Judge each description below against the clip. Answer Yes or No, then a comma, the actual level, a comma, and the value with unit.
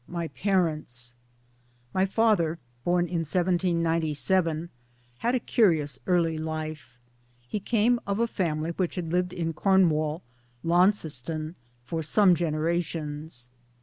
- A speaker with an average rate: No, slow, 115 wpm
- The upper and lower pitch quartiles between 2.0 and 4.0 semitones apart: Yes, average, 2.9 semitones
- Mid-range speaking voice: Yes, medium, 170 Hz